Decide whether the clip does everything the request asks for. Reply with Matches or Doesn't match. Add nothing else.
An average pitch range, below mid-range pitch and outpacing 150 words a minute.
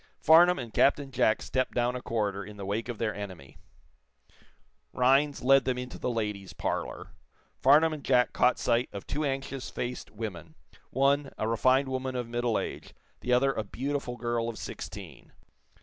Matches